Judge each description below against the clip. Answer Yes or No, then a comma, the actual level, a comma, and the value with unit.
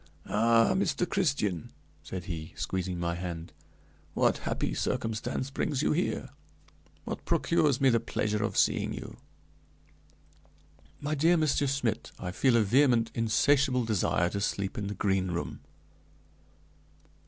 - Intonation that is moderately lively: No, wide, 6.7 semitones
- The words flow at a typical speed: No, slow, 130 wpm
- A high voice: No, low, 115 Hz